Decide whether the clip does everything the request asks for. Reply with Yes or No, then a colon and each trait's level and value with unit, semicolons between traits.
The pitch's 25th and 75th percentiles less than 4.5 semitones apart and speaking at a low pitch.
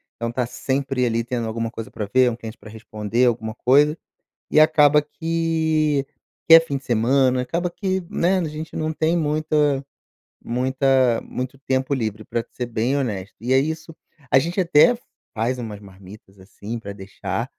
No: average, 5.0 semitones; low, 130 Hz